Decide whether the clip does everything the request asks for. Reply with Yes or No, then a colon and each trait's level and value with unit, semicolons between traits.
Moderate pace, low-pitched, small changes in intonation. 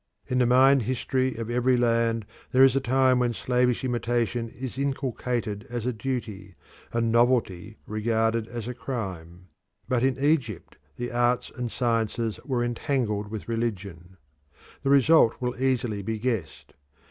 Yes: average, 145 wpm; low, 120 Hz; narrow, 2.3 semitones